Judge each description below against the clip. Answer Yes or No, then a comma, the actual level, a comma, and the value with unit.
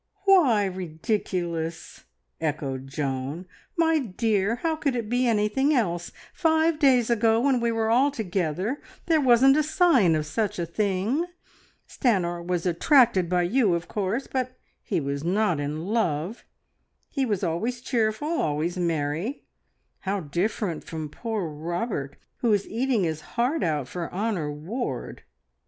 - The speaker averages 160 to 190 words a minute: No, average, 145 wpm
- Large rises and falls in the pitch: Yes, wide, 6.7 semitones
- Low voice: No, high, 205 Hz